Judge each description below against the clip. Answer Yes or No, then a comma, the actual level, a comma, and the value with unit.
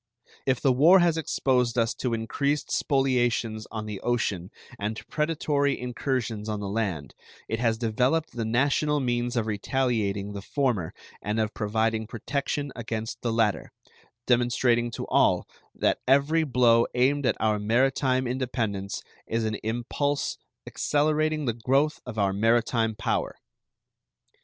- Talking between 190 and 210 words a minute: No, average, 140 wpm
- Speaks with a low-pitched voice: Yes, low, 120 Hz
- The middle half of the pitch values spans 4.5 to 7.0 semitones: No, average, 3.5 semitones